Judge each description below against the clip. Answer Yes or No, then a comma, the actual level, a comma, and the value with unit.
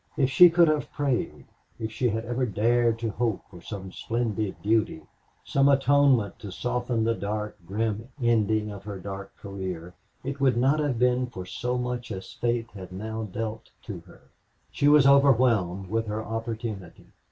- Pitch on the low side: Yes, low, 115 Hz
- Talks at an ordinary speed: Yes, average, 170 wpm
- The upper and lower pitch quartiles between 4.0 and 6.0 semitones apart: No, average, 3.3 semitones